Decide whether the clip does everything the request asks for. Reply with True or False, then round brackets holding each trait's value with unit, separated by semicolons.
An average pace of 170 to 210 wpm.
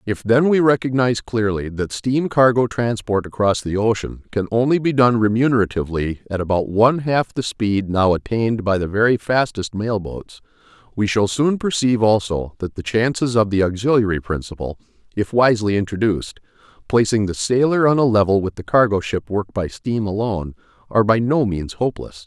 True (175 wpm)